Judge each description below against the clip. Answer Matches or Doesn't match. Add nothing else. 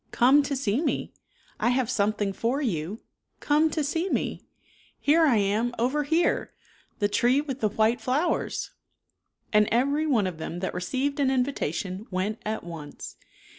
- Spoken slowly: Doesn't match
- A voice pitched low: Doesn't match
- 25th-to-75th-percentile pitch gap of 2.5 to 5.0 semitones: Doesn't match